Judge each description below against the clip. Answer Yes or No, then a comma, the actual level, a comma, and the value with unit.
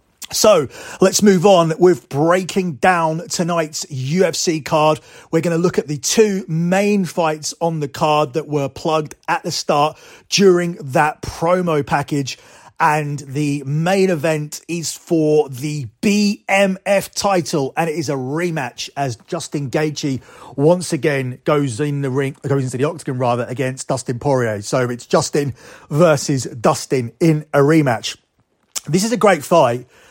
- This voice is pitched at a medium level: Yes, medium, 155 Hz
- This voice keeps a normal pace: Yes, average, 150 wpm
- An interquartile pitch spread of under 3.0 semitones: No, average, 3.8 semitones